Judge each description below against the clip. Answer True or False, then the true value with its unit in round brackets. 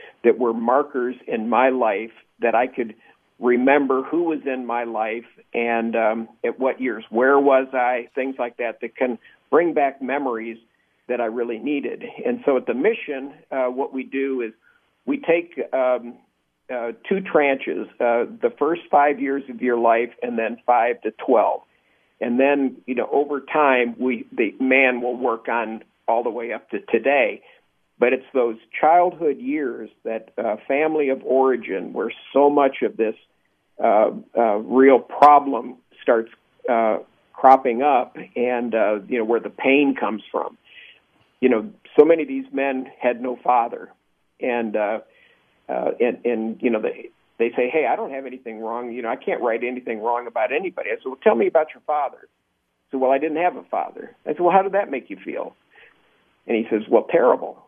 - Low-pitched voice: True (130 Hz)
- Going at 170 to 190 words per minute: True (185 wpm)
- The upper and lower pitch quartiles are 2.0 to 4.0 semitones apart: True (3.4 semitones)